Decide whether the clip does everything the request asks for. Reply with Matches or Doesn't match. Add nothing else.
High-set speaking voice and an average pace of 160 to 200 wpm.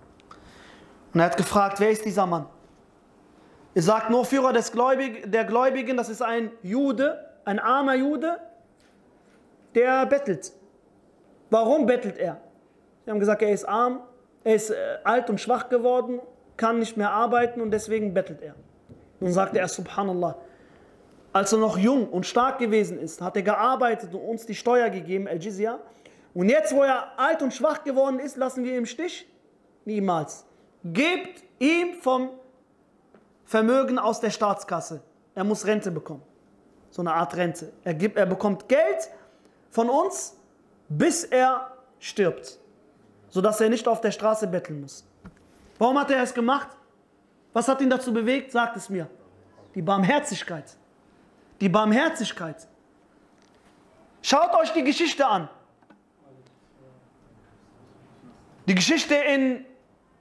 Doesn't match